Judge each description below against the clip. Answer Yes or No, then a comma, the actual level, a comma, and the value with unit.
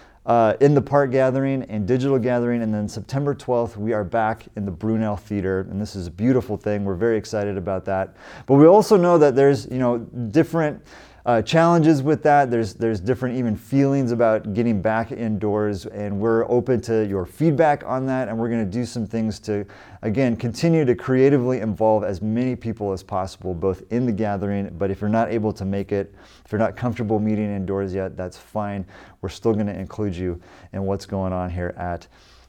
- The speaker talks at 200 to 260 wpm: Yes, fast, 205 wpm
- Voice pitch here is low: Yes, low, 110 Hz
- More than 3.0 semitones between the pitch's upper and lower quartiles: Yes, average, 4.1 semitones